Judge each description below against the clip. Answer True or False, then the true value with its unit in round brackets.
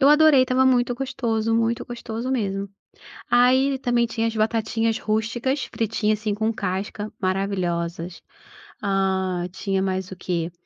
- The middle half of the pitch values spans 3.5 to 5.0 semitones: True (4.0 semitones)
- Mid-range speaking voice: False (220 Hz)